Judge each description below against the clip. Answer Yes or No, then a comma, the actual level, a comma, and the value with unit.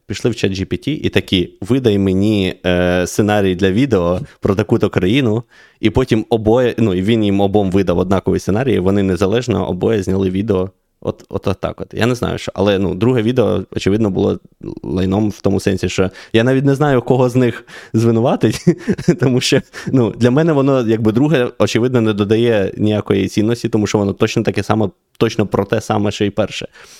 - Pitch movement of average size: Yes, average, 3.5 semitones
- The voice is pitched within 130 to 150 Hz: No, low, 105 Hz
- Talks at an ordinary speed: No, fast, 190 wpm